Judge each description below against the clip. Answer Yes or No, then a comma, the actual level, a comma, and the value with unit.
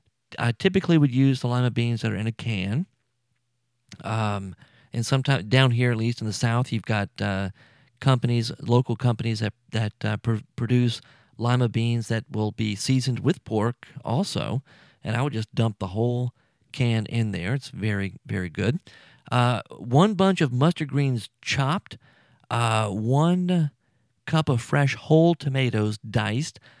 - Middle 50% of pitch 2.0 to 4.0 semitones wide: Yes, average, 3.3 semitones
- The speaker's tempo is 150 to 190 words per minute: Yes, average, 160 wpm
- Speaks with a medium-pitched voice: No, low, 120 Hz